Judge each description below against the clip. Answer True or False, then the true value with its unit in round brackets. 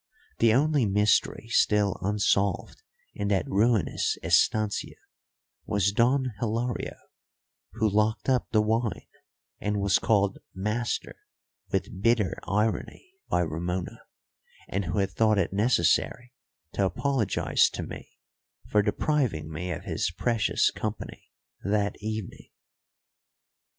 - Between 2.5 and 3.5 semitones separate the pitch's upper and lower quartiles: True (3.0 semitones)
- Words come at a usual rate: False (115 wpm)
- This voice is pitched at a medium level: False (105 Hz)